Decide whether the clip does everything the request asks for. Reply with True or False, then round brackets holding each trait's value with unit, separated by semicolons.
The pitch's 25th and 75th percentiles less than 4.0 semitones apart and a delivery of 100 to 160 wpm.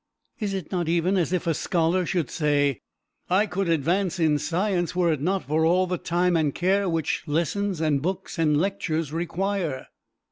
False (2.9 semitones; 180 wpm)